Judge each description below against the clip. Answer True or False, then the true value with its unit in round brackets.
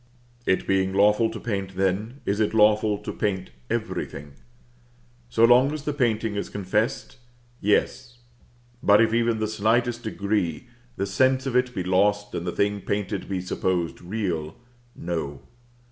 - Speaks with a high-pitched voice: False (105 Hz)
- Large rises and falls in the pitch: False (3.3 semitones)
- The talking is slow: False (155 wpm)